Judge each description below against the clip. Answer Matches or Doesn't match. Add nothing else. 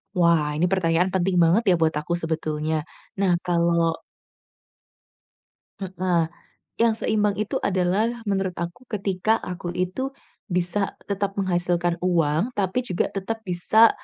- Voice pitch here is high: Doesn't match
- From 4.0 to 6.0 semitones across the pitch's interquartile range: Doesn't match